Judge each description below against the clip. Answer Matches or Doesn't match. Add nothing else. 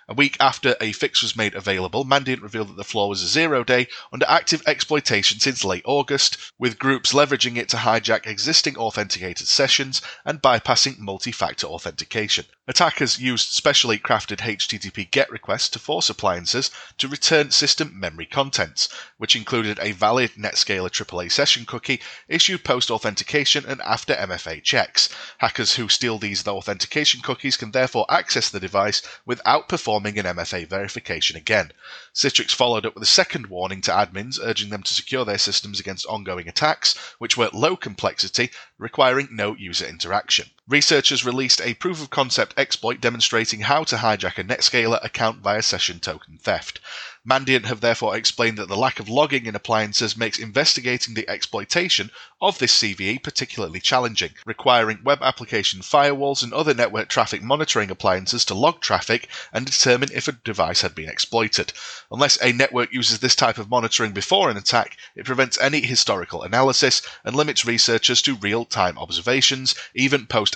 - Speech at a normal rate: Matches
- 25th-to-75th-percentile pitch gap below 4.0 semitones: Doesn't match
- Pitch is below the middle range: Matches